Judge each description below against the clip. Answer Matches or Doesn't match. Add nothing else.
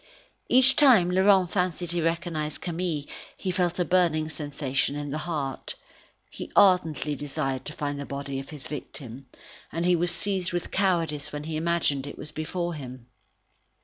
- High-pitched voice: Doesn't match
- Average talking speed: Matches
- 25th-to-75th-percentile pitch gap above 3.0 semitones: Matches